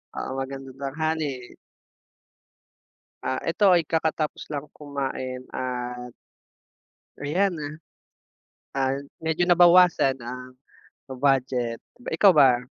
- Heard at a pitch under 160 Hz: Yes, low, 135 Hz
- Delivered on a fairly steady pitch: No, average, 3.8 semitones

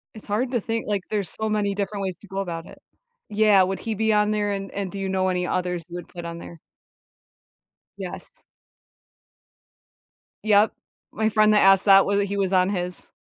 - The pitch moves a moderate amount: No, narrow, 2.2 semitones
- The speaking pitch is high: Yes, high, 200 Hz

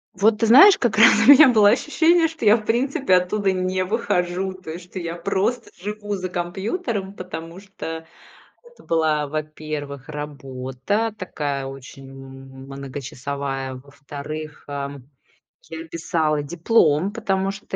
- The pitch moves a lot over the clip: Yes, wide, 6.4 semitones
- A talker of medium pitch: Yes, medium, 175 Hz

